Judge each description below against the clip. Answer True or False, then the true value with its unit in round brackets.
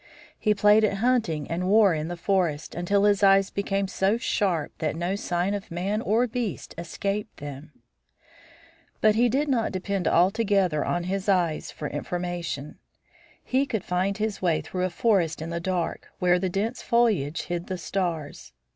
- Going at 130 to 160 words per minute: False (170 wpm)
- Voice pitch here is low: False (190 Hz)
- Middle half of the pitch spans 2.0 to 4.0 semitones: True (3.5 semitones)